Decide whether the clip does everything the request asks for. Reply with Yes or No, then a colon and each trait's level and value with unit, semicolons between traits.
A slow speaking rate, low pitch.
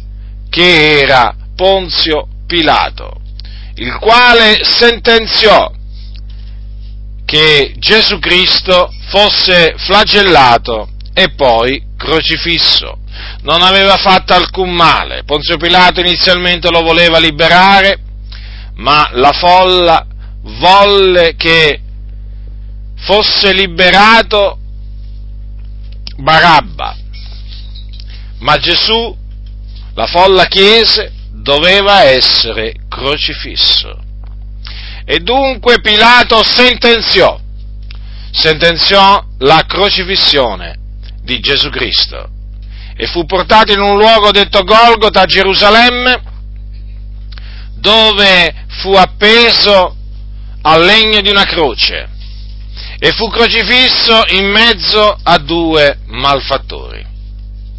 No: slow, 80 wpm; medium, 160 Hz